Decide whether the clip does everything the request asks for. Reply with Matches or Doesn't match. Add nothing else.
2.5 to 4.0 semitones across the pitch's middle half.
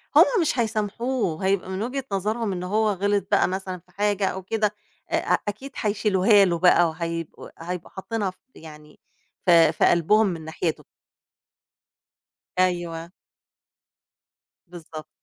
Matches